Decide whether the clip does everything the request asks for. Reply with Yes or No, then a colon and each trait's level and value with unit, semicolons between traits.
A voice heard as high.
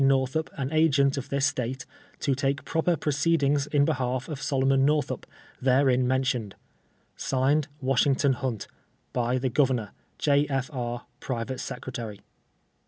No: low, 135 Hz